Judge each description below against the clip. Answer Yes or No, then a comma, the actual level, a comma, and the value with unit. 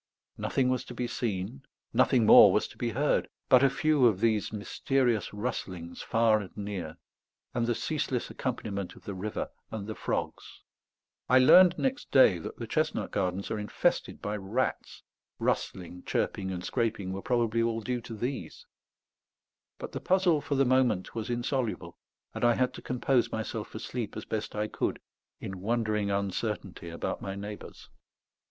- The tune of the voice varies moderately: Yes, average, 4.0 semitones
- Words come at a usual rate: Yes, average, 165 wpm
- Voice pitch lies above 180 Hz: No, low, 110 Hz